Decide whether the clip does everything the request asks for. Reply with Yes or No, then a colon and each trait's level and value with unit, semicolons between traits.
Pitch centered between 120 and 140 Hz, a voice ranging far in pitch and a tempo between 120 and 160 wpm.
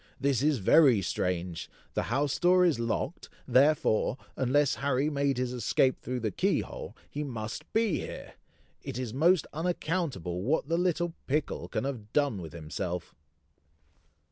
Yes: low, 135 Hz; wide, 5.7 semitones; average, 150 wpm